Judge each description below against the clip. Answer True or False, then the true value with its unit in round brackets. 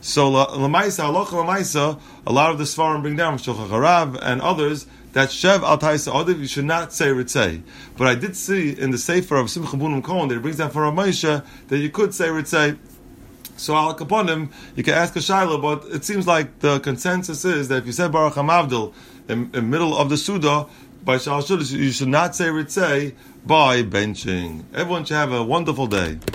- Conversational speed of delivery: True (185 wpm)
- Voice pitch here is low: False (150 Hz)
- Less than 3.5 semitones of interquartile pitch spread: False (3.9 semitones)